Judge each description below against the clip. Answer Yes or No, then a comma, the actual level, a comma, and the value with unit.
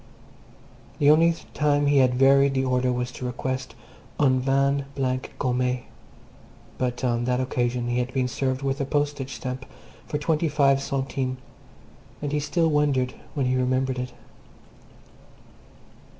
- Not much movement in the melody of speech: Yes, narrow, 1.9 semitones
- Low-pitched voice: Yes, low, 130 Hz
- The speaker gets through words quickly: No, average, 145 wpm